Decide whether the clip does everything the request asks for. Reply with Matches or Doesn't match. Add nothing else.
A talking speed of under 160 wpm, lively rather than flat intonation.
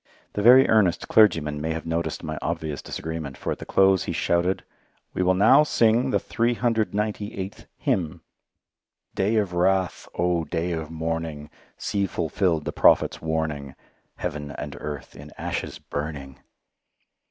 Doesn't match